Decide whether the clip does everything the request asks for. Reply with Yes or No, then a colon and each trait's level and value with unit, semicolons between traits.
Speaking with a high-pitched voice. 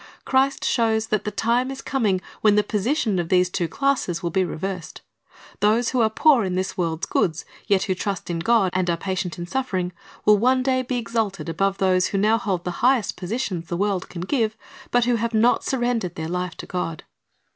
Yes: high, 200 Hz